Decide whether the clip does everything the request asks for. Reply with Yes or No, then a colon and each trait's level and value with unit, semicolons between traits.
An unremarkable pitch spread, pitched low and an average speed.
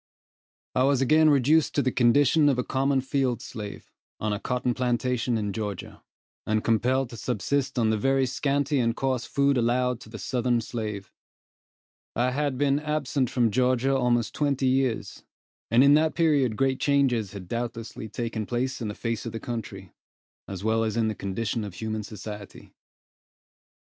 Yes: average, 3.4 semitones; low, 125 Hz; average, 170 wpm